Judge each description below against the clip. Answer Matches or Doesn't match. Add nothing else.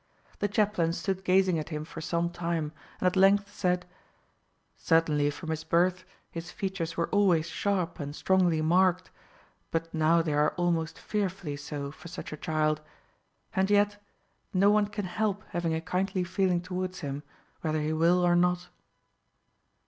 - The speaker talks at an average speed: Matches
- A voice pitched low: Doesn't match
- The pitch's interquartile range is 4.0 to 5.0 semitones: Doesn't match